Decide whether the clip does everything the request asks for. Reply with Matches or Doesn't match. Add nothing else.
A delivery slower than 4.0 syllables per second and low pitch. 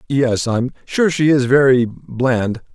Matches